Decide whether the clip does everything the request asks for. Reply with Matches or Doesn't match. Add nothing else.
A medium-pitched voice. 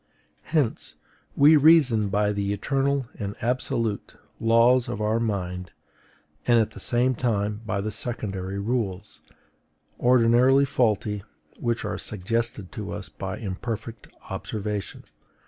Doesn't match